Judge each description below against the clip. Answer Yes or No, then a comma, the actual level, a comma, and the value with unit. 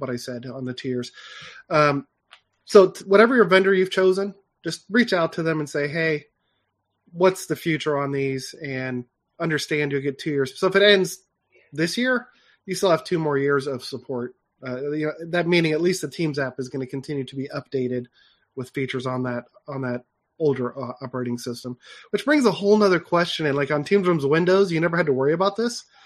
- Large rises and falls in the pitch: Yes, wide, 5.8 semitones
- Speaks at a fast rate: Yes, fast, 215 wpm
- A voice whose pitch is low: No, medium, 150 Hz